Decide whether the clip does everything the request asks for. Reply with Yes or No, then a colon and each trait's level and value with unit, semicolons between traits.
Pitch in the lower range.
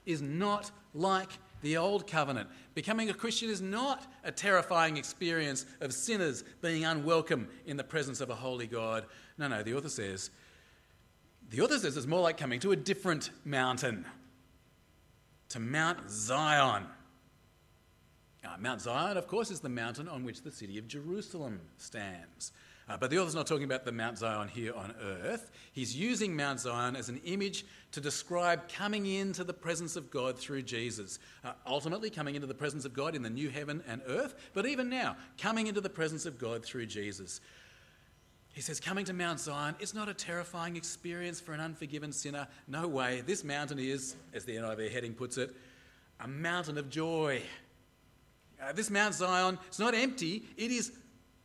No: medium, 150 Hz